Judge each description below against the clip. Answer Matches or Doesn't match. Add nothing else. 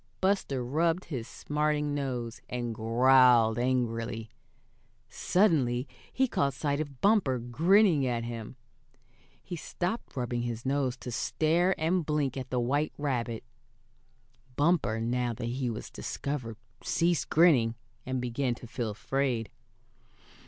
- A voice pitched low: Matches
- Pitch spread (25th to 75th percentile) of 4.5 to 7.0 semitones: Doesn't match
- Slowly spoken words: Matches